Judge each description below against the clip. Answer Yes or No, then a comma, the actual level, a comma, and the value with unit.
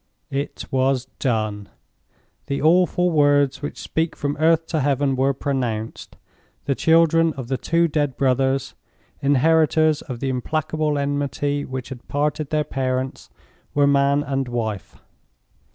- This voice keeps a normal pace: No, slow, 125 wpm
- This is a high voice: No, medium, 140 Hz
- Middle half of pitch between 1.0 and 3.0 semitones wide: Yes, average, 2.7 semitones